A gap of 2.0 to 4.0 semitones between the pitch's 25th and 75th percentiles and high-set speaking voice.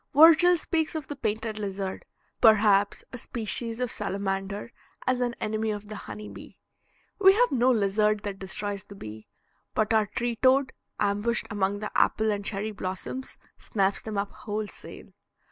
Yes: average, 3.2 semitones; high, 215 Hz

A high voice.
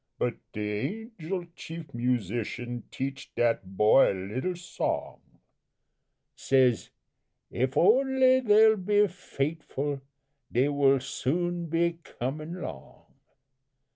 No: medium, 140 Hz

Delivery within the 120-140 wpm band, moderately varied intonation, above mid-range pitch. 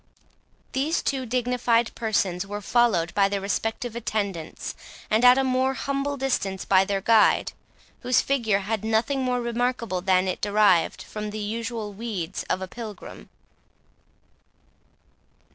Yes: slow, 135 wpm; average, 3.9 semitones; high, 220 Hz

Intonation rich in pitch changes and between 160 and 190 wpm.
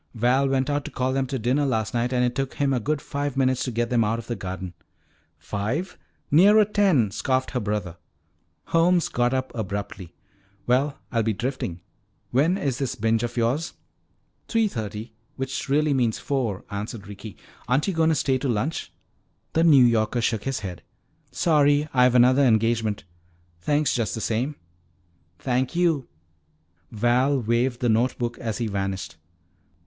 No: average, 3.8 semitones; average, 170 wpm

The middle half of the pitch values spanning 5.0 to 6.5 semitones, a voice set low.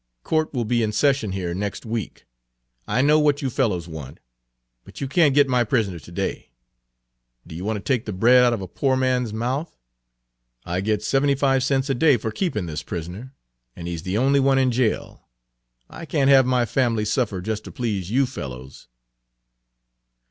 Yes: average, 5.3 semitones; low, 120 Hz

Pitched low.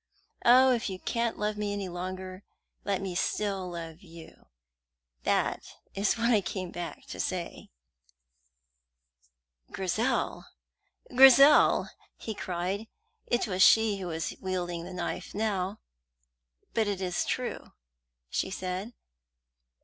No: high, 190 Hz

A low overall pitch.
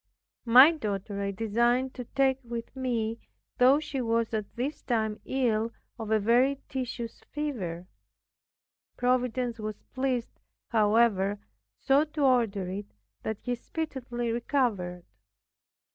No: high, 235 Hz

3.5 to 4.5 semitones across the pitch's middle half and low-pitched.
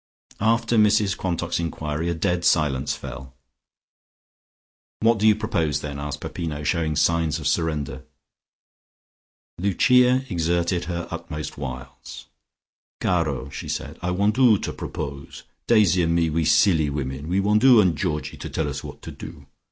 No: average, 5.0 semitones; very low, 85 Hz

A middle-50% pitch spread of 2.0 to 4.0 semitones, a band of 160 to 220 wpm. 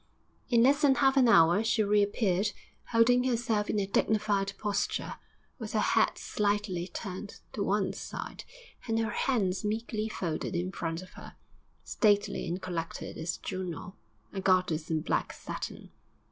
No: average, 3.4 semitones; average, 150 wpm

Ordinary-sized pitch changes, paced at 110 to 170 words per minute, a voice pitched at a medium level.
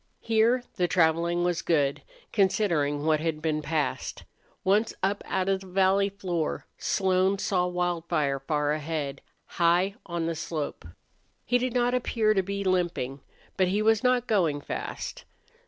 Yes: average, 3.8 semitones; average, 150 wpm; medium, 180 Hz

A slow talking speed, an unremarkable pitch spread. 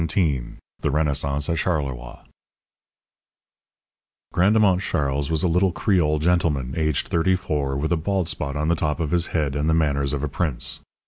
No: average, 170 wpm; average, 3.5 semitones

